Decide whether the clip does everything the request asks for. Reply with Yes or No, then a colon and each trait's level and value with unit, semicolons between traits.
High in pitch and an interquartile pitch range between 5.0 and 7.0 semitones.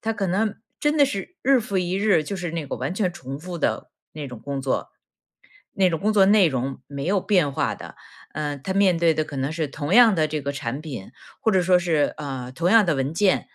No: medium, 170 Hz; wide, 5.5 semitones